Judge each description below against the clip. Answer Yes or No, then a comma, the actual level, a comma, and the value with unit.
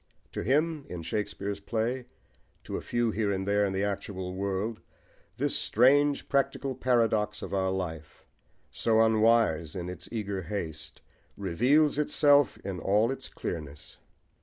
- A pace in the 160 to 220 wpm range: No, average, 140 wpm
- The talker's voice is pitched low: Yes, low, 105 Hz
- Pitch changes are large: No, average, 4.2 semitones